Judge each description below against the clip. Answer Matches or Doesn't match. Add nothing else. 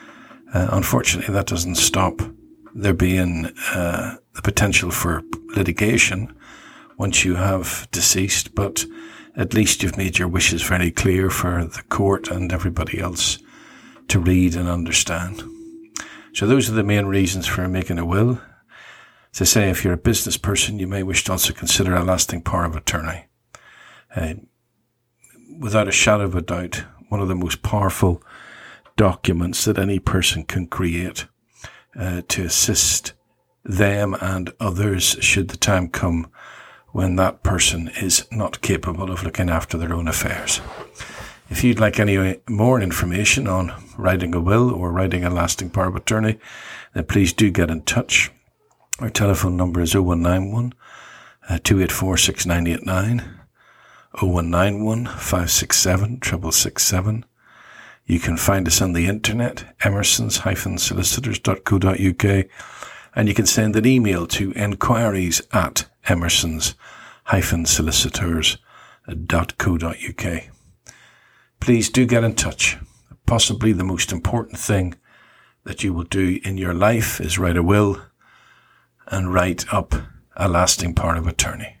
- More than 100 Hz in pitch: Doesn't match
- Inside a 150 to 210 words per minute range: Doesn't match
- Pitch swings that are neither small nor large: Matches